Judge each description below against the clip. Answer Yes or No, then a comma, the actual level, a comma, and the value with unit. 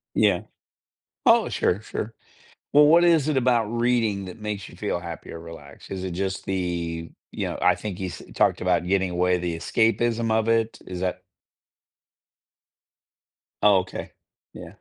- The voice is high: No, low, 100 Hz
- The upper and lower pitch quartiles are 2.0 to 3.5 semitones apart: No, average, 4.3 semitones